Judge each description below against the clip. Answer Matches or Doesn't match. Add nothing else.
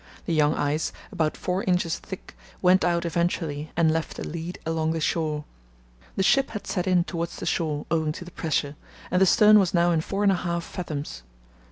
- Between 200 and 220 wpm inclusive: Matches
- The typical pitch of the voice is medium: Matches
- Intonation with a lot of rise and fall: Doesn't match